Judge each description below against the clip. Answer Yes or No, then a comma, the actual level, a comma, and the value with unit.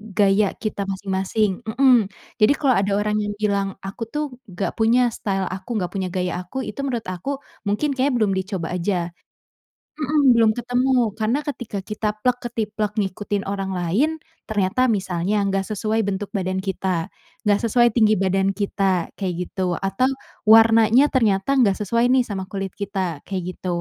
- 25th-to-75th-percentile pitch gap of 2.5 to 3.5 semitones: Yes, average, 3.2 semitones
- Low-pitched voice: No, high, 205 Hz